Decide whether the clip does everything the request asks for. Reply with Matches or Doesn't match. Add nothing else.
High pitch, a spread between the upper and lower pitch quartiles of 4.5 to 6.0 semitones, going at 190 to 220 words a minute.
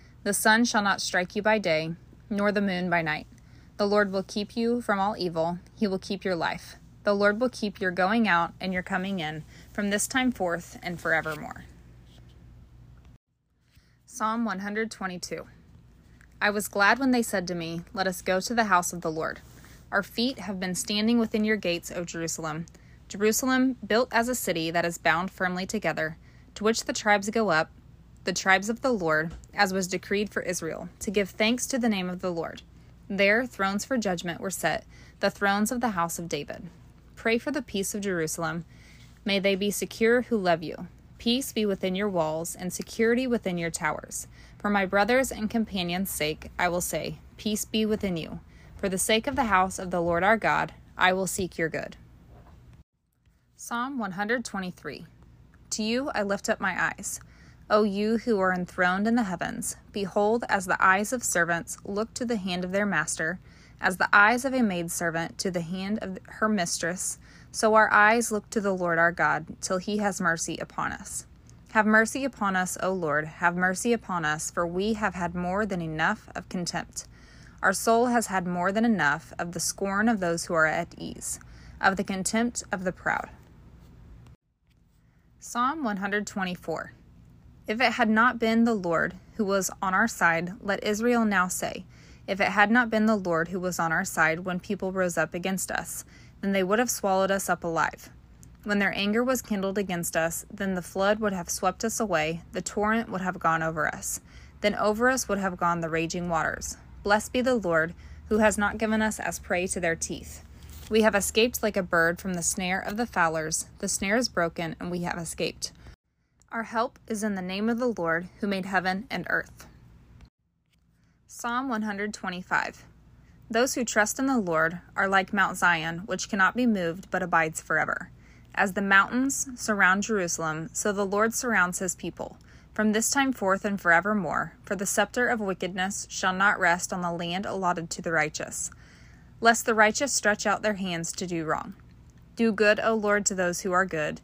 Doesn't match